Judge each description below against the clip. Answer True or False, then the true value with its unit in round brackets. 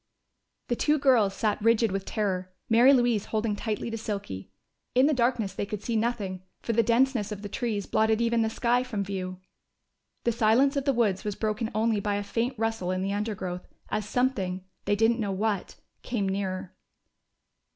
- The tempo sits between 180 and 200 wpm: True (190 wpm)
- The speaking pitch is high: True (215 Hz)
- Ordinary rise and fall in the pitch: True (3.0 semitones)